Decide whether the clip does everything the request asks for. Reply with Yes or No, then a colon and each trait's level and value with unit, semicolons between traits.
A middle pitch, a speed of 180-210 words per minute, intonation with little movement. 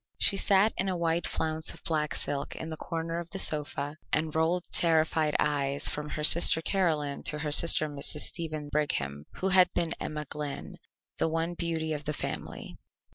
Yes: medium, 160 Hz; average, 185 wpm; narrow, 2.0 semitones